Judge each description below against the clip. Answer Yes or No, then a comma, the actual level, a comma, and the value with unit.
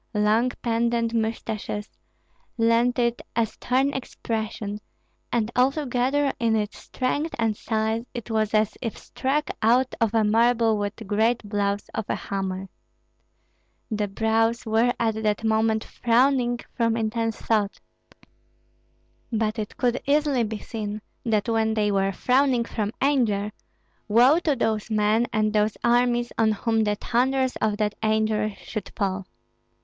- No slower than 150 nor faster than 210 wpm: No, slow, 135 wpm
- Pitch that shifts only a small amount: Yes, narrow, 2.1 semitones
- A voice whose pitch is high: Yes, high, 225 Hz